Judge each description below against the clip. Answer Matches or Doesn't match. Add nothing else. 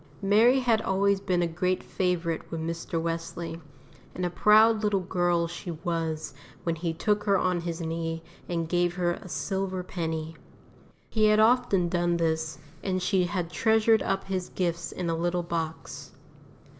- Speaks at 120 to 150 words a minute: Doesn't match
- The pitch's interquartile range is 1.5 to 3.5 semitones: Matches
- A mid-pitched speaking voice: Matches